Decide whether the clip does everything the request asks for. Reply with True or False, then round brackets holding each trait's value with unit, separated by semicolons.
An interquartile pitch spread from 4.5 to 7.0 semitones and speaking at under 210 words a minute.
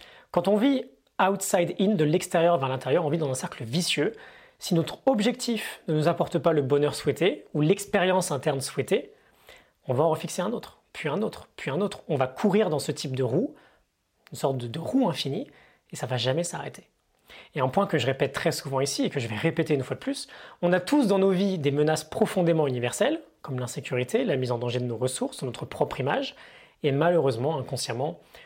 False (5.6 semitones; 215 wpm)